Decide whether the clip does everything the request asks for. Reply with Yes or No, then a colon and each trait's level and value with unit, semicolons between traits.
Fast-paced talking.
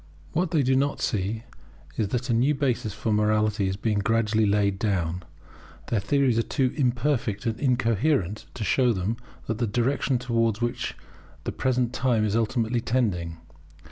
No: average, 160 wpm